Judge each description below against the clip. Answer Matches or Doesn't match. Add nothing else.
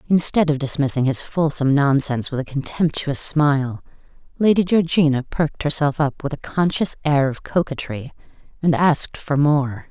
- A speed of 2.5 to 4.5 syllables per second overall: Doesn't match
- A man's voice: Doesn't match